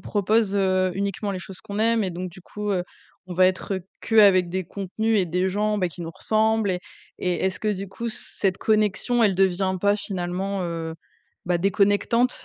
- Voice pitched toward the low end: No, high, 195 Hz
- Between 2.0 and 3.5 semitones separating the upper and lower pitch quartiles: Yes, narrow, 2.4 semitones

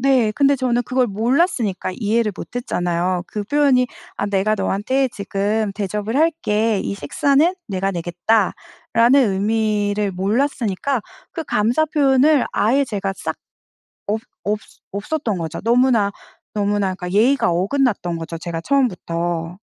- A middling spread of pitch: Yes, average, 4.9 semitones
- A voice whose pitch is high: Yes, high, 215 Hz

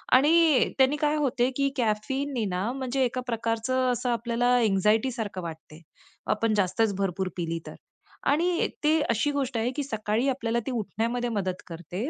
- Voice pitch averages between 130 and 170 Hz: No, high, 235 Hz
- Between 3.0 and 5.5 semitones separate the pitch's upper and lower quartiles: Yes, average, 4.0 semitones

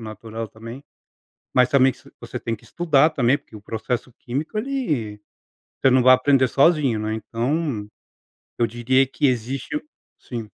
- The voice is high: No, low, 125 Hz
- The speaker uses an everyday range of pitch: Yes, average, 3.6 semitones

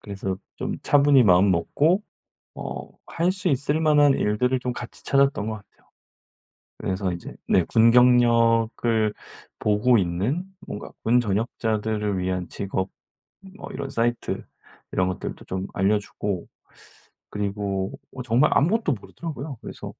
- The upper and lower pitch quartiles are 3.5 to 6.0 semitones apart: Yes, average, 5.2 semitones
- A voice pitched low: Yes, low, 115 Hz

